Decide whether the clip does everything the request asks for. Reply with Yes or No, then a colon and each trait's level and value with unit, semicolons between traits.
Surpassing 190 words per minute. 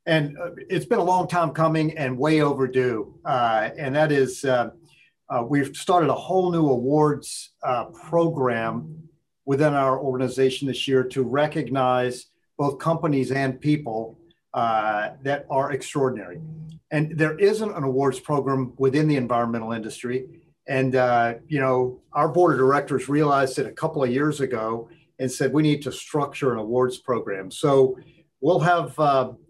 No: average, 155 wpm